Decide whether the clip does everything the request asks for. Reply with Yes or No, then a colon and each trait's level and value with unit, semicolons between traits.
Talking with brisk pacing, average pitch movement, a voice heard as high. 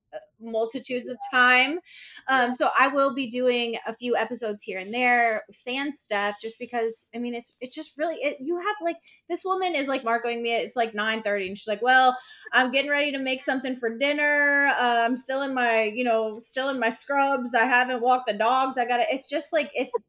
Yes: fast, 220 wpm; average, 3.2 semitones; very high, 250 Hz